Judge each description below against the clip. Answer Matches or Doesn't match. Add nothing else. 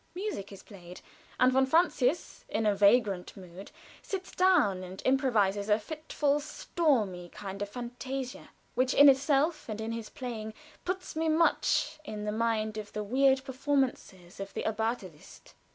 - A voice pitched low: Doesn't match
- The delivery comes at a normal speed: Matches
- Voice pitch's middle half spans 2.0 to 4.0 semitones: Doesn't match